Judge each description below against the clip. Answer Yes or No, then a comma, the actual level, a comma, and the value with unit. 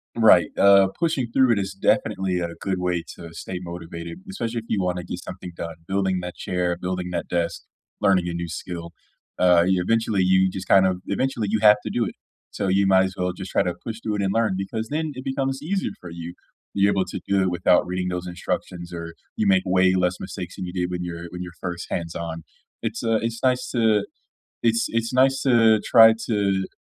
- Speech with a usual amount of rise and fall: Yes, average, 4.0 semitones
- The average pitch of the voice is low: Yes, very low, 95 Hz